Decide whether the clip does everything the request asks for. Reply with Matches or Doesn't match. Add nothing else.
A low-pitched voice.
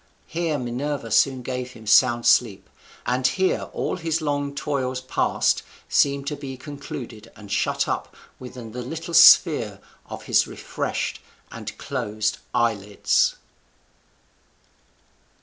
Matches